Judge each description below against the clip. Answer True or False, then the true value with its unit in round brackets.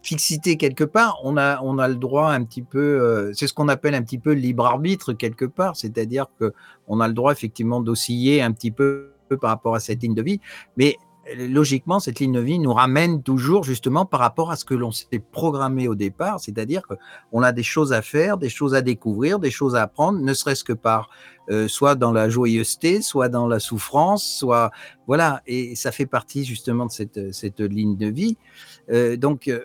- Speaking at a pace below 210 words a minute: False (215 wpm)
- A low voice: True (130 Hz)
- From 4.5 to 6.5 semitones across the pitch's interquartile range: False (3.7 semitones)